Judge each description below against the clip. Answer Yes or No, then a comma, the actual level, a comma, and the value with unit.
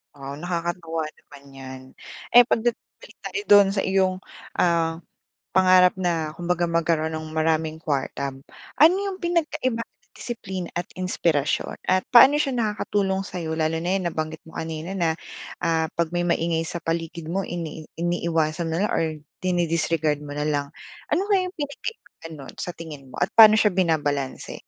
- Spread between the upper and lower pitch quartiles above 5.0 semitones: No, average, 3.4 semitones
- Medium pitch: Yes, medium, 170 Hz